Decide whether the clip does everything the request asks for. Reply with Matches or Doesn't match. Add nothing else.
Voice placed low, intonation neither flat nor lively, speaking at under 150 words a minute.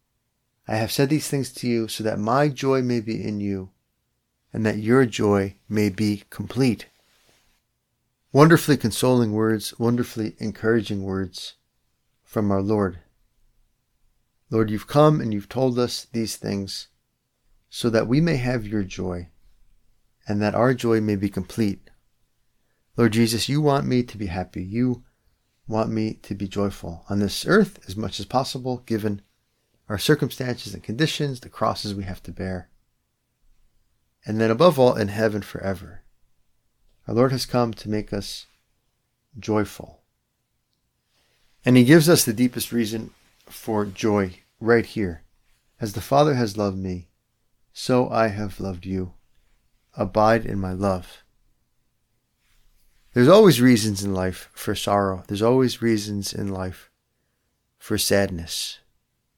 Matches